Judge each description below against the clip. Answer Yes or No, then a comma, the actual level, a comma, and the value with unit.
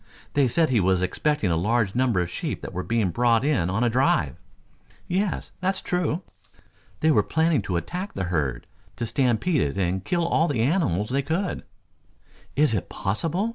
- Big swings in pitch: Yes, wide, 9.0 semitones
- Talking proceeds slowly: No, average, 190 wpm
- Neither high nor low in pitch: No, low, 120 Hz